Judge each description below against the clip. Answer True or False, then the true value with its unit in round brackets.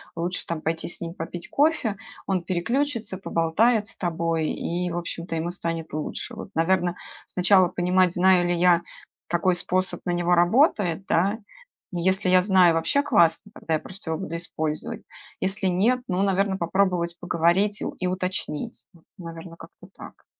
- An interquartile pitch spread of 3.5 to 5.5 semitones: False (2.4 semitones)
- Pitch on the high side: False (180 Hz)